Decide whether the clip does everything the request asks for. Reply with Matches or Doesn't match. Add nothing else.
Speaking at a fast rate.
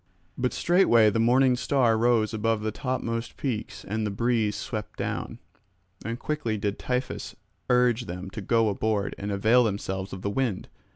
Doesn't match